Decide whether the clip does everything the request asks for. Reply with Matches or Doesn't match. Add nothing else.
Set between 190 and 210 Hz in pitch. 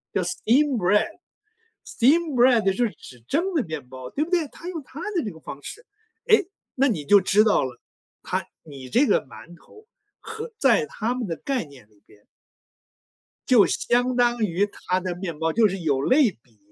Doesn't match